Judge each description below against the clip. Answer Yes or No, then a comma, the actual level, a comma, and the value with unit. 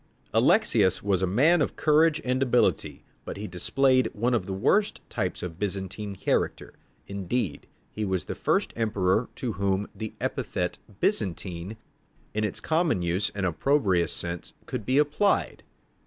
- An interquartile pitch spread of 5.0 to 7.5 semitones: Yes, wide, 5.5 semitones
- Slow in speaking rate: No, average, 145 wpm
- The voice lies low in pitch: Yes, low, 105 Hz